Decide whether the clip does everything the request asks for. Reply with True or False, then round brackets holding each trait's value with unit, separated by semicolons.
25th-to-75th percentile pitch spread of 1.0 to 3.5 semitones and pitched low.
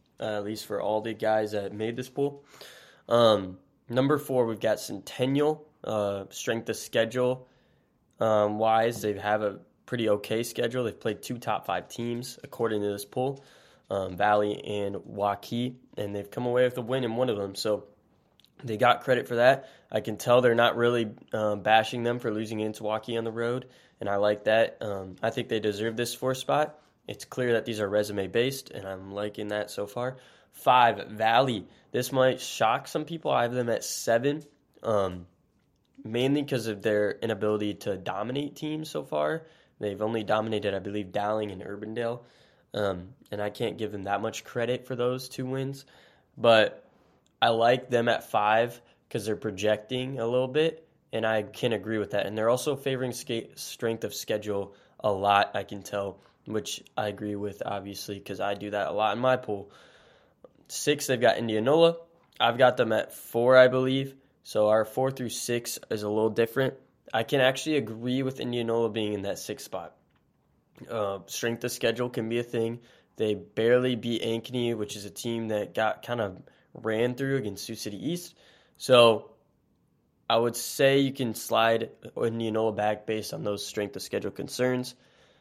True (3.2 semitones; 115 Hz)